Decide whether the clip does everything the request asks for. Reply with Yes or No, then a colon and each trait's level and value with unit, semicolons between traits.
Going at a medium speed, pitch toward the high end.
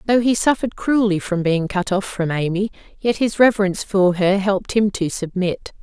Yes: average, 195 wpm; high, 200 Hz